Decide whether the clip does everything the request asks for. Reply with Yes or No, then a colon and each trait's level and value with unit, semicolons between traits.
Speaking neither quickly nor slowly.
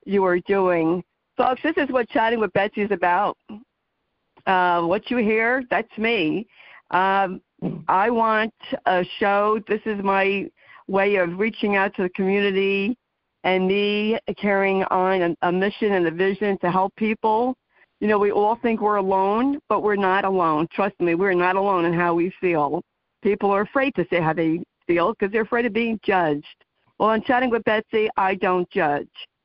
Yes: average, 180 wpm